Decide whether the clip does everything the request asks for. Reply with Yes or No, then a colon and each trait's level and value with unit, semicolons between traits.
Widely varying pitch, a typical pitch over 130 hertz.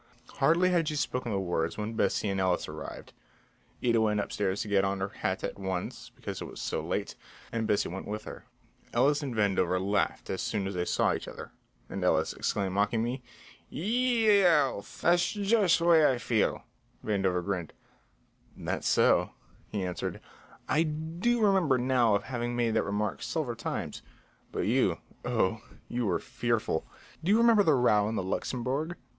No: wide, 8.0 semitones; low, 115 Hz